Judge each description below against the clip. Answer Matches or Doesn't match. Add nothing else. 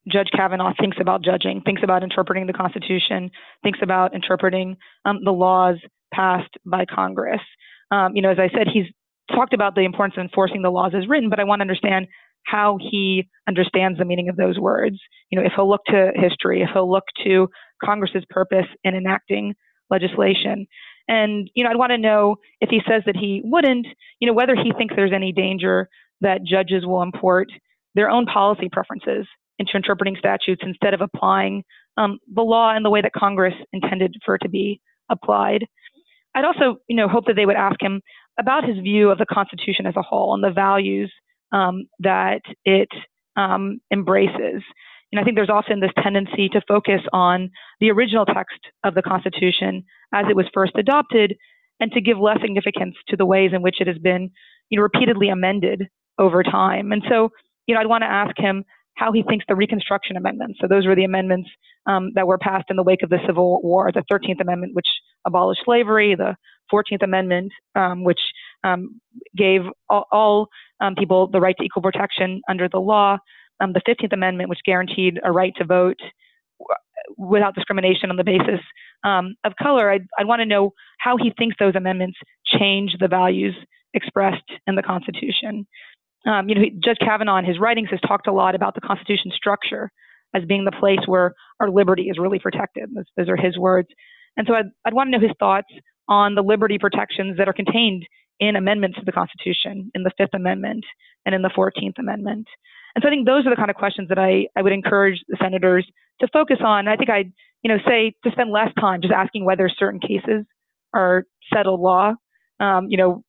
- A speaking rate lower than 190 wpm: Doesn't match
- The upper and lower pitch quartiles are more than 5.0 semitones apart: Doesn't match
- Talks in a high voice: Matches